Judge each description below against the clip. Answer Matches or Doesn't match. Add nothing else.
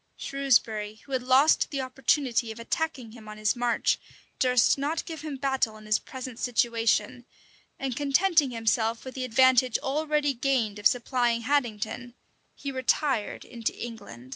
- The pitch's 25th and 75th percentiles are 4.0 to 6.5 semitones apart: Doesn't match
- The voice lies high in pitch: Matches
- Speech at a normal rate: Matches